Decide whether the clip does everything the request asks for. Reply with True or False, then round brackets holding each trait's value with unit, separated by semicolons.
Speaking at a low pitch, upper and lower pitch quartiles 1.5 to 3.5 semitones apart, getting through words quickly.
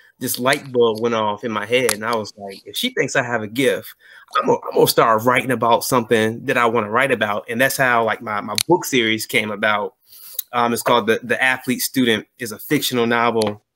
True (120 Hz; 2.9 semitones; 235 wpm)